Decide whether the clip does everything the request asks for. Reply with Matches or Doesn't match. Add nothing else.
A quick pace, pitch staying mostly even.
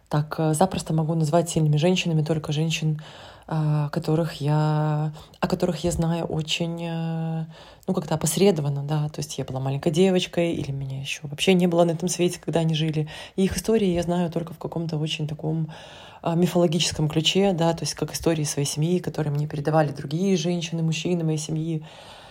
Matches